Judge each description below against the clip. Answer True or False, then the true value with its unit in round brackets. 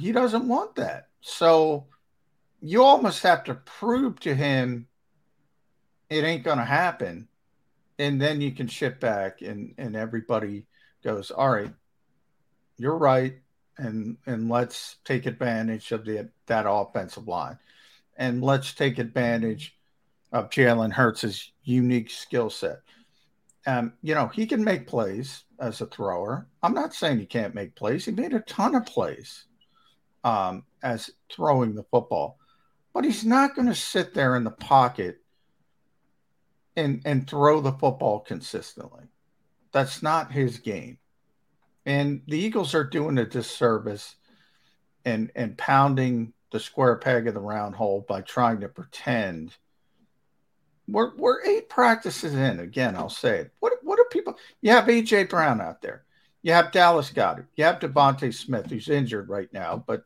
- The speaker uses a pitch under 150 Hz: True (135 Hz)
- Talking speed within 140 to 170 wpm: True (150 wpm)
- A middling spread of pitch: False (6.6 semitones)